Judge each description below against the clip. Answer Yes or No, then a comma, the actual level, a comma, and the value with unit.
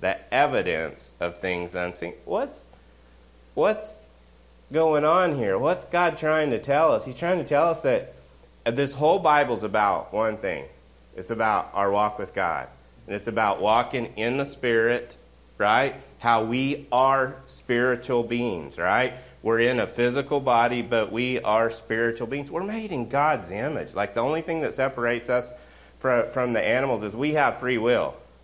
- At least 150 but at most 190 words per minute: Yes, average, 165 wpm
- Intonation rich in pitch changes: Yes, wide, 6.9 semitones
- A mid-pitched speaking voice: No, low, 120 Hz